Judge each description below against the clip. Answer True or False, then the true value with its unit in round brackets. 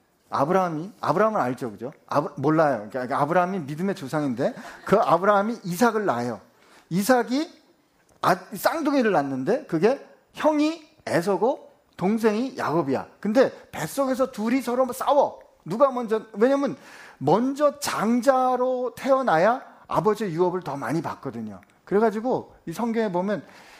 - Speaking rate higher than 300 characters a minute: True (310 characters per minute)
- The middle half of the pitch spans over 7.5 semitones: True (8.5 semitones)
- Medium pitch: False (215 Hz)